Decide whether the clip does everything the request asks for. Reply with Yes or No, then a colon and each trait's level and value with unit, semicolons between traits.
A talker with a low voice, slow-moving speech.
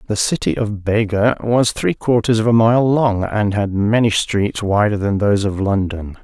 No: low, 105 Hz; average, 190 wpm